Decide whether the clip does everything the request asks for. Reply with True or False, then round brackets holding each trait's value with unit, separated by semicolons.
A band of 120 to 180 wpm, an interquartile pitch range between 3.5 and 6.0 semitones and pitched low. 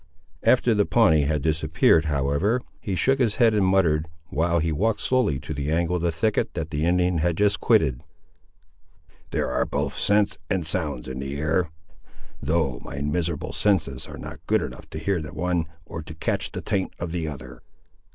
False (190 wpm; 4.1 semitones; 80 Hz)